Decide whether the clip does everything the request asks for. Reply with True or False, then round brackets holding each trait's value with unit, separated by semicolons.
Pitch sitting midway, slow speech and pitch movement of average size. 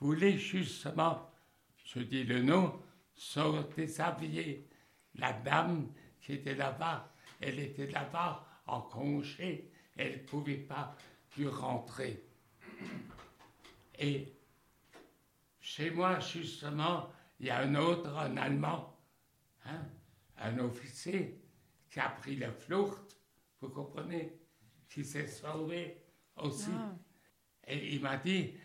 True (150 Hz; 110 wpm; 3.8 semitones)